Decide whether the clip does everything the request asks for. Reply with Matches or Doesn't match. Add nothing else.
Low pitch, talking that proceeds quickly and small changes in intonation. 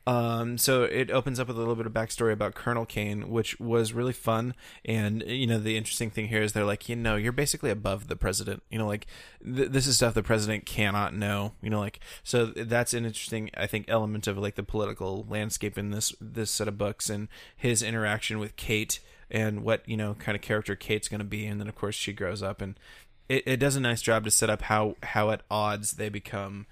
Matches